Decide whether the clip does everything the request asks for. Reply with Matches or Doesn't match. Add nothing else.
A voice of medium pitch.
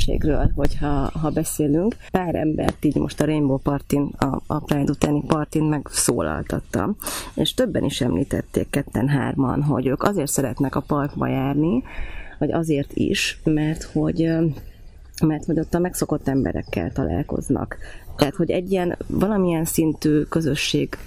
Matches